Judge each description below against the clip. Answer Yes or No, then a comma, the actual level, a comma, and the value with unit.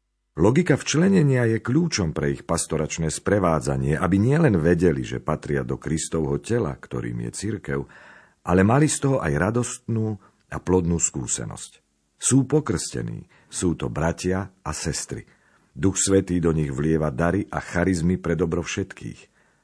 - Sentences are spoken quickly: No, average, 140 wpm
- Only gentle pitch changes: No, wide, 6.1 semitones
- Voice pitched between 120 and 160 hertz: No, very low, 90 Hz